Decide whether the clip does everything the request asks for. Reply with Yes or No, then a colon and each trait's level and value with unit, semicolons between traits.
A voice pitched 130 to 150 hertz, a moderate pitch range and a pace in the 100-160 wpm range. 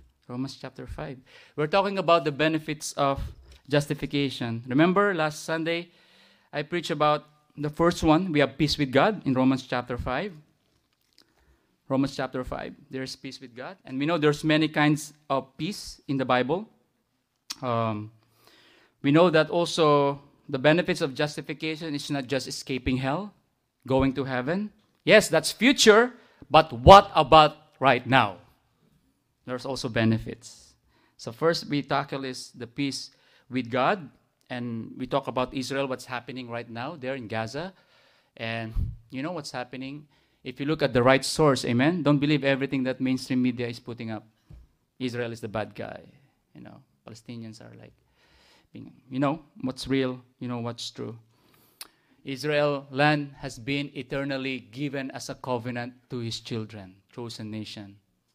Yes: low, 135 Hz; average, 3.4 semitones; average, 155 wpm